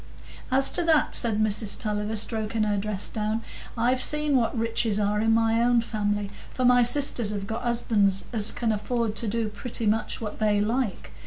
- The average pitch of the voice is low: No, high, 225 Hz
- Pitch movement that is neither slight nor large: No, narrow, 2.2 semitones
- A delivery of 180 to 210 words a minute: Yes, average, 185 wpm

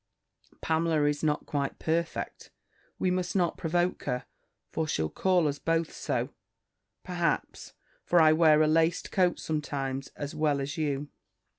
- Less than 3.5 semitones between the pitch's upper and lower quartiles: Yes, narrow, 2.6 semitones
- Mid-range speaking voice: Yes, medium, 155 Hz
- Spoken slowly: No, average, 145 wpm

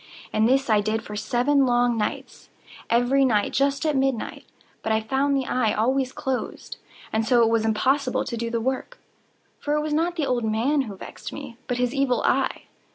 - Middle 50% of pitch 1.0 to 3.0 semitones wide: No, average, 3.6 semitones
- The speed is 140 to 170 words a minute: No, average, 190 wpm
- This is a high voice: Yes, very high, 250 Hz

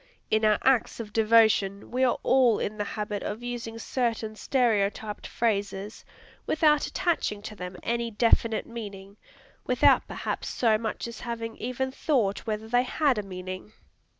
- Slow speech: No, average, 150 wpm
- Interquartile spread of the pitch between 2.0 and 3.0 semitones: Yes, narrow, 2.5 semitones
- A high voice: Yes, high, 225 Hz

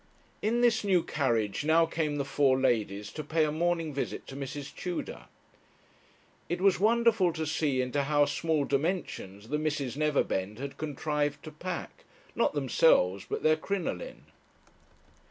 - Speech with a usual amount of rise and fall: Yes, average, 3.5 semitones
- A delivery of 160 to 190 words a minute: No, average, 150 wpm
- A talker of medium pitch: Yes, medium, 150 Hz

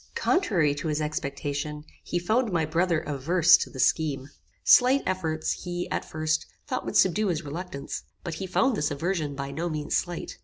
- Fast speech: No, average, 180 wpm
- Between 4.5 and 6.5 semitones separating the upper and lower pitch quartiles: No, average, 3.5 semitones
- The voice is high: No, medium, 160 Hz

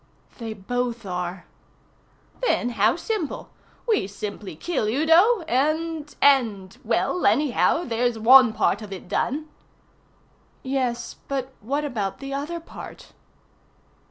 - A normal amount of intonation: No, wide, 5.8 semitones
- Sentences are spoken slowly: Yes, slow, 115 wpm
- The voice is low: No, very high, 250 Hz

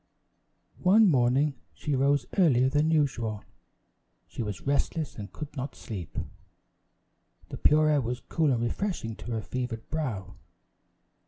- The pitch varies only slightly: No, average, 4.7 semitones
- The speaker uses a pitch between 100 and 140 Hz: Yes, low, 135 Hz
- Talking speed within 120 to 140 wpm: Yes, slow, 135 wpm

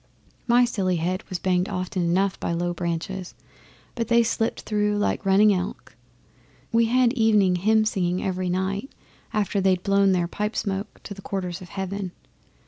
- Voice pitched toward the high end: Yes, high, 195 Hz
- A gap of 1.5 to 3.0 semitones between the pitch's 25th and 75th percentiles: Yes, narrow, 2.6 semitones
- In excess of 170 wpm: No, average, 165 wpm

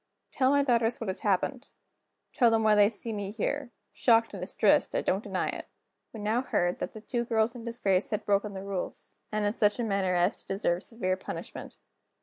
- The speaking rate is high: Yes, fast, 210 wpm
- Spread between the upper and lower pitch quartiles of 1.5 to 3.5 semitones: Yes, average, 3.0 semitones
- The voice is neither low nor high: No, high, 215 Hz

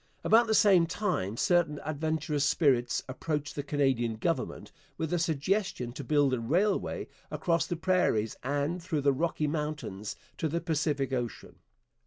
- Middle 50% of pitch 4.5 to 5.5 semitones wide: No, average, 4.0 semitones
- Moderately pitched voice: Yes, medium, 150 Hz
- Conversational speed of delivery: Yes, average, 150 wpm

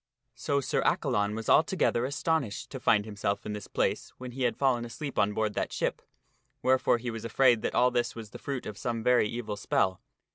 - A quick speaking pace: Yes, fast, 210 wpm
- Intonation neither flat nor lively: Yes, average, 3.4 semitones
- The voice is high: No, low, 120 Hz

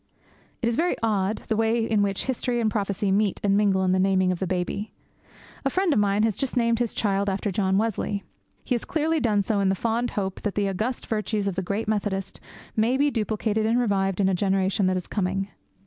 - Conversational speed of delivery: No, fast, 225 wpm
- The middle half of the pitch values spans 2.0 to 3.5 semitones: Yes, average, 2.8 semitones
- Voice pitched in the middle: No, high, 205 Hz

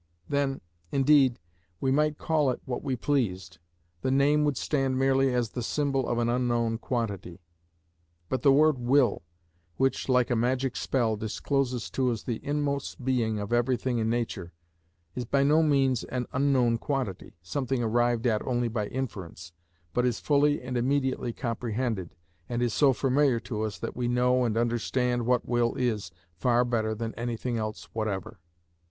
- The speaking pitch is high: No, low, 125 Hz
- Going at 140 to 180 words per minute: Yes, average, 165 wpm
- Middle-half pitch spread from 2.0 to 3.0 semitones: Yes, average, 2.7 semitones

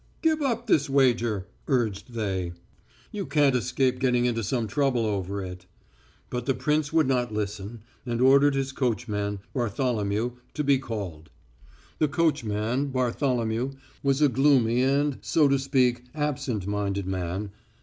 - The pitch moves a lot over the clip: No, average, 4.7 semitones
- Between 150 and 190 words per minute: No, average, 140 wpm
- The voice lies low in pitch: Yes, low, 125 Hz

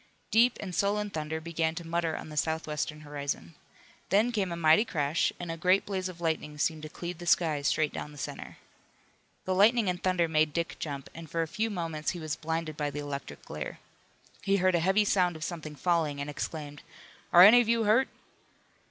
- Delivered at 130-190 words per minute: No, fast, 205 wpm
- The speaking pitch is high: No, medium, 165 Hz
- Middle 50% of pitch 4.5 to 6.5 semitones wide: No, average, 3.4 semitones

